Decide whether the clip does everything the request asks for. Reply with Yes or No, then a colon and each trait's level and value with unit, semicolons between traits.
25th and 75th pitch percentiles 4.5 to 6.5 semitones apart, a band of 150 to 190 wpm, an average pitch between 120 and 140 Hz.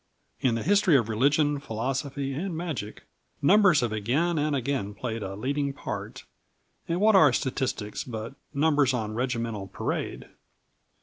No: average, 4.8 semitones; average, 140 wpm; low, 135 Hz